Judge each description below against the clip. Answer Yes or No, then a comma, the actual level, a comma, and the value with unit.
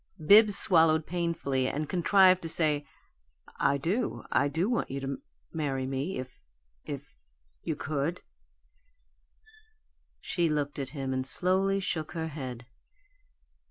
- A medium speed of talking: No, slow, 125 wpm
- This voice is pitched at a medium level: Yes, medium, 155 Hz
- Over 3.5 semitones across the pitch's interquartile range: Yes, average, 4.6 semitones